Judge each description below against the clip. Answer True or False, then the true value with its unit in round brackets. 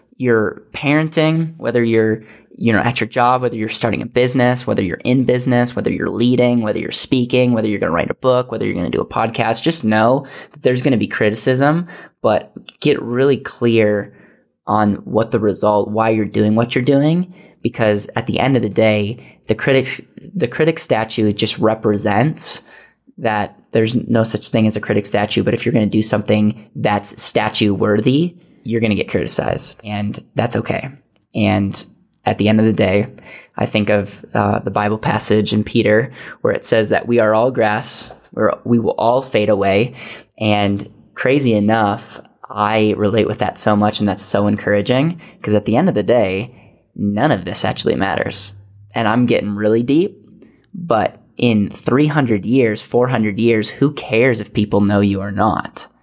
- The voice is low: True (110 Hz)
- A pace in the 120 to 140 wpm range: False (185 wpm)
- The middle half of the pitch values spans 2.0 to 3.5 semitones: True (2.9 semitones)